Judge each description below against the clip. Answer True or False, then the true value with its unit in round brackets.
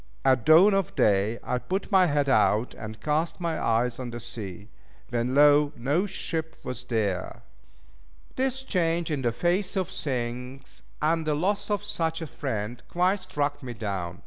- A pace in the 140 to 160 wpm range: False (170 wpm)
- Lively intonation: True (6.5 semitones)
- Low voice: False (145 Hz)